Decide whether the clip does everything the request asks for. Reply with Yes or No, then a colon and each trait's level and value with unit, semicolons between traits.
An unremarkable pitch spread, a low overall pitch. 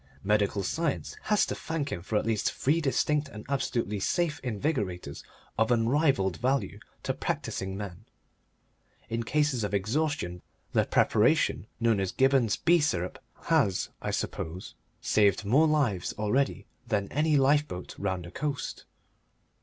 No: wide, 6.6 semitones; low, 115 Hz